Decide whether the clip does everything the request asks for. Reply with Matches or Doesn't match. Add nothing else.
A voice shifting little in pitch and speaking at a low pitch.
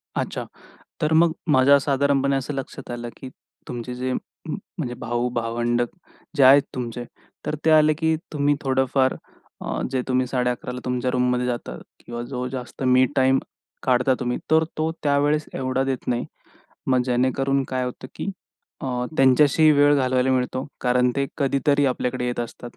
Matches